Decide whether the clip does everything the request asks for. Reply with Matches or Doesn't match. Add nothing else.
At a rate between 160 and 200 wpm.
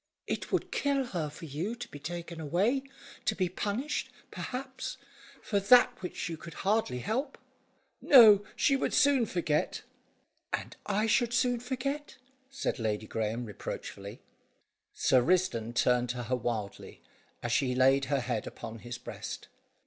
Doesn't match